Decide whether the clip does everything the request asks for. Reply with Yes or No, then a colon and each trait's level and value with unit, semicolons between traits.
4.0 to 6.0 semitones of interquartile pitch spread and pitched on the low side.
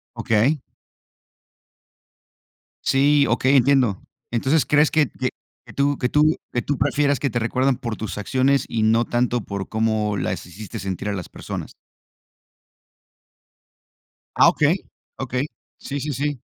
Yes: average, 4.3 semitones; low, 130 Hz